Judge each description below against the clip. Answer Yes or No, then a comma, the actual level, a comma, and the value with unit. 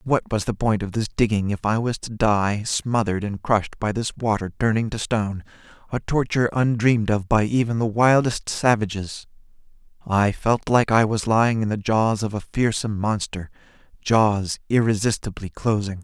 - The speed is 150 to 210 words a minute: Yes, average, 170 wpm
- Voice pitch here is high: No, low, 110 Hz